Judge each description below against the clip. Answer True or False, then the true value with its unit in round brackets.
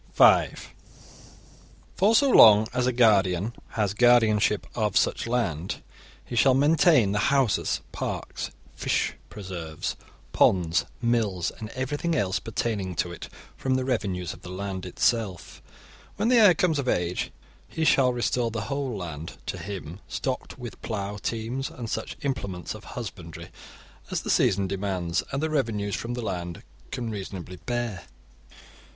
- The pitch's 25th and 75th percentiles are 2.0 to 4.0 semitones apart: False (5.2 semitones)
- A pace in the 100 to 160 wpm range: True (145 wpm)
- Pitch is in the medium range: False (110 Hz)